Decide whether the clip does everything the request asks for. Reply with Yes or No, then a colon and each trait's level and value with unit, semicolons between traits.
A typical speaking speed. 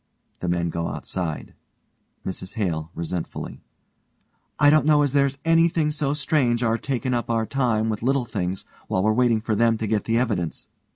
Yes: average, 175 wpm